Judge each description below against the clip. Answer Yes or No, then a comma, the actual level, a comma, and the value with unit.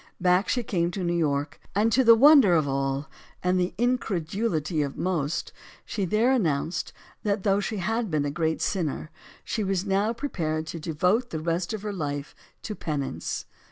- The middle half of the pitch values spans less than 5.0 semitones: No, average, 5.3 semitones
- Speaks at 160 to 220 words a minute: Yes, average, 180 wpm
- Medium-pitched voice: Yes, medium, 180 Hz